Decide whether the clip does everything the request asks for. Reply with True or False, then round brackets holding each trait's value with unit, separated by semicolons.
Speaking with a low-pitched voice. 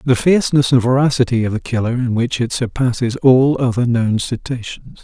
True (125 Hz)